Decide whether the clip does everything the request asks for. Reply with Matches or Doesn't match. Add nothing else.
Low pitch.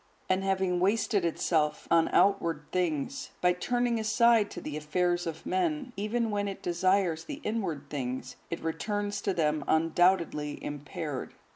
Doesn't match